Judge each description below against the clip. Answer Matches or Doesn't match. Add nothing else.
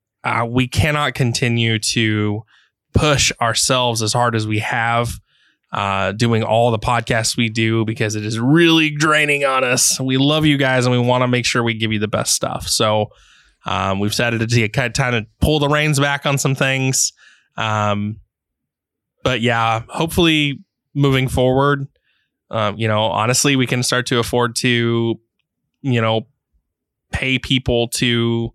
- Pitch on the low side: Matches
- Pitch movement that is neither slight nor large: Matches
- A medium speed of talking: Matches